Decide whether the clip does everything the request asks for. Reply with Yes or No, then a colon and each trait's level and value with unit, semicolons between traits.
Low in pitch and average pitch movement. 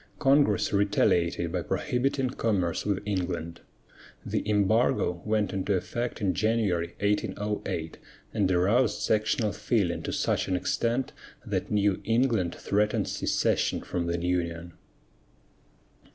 Yes: low, 100 Hz; average, 3.8 semitones